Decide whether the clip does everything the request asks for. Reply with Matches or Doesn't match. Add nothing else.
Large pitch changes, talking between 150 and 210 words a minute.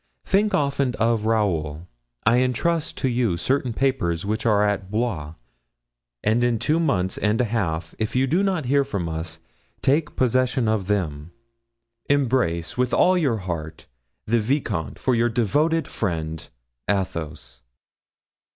Doesn't match